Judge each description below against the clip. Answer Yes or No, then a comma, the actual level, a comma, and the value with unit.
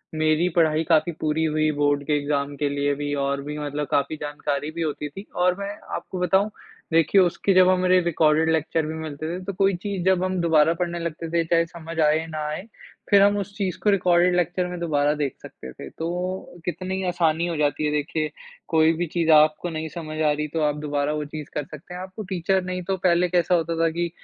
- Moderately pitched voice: Yes, medium, 165 Hz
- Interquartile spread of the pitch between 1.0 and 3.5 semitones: Yes, average, 2.9 semitones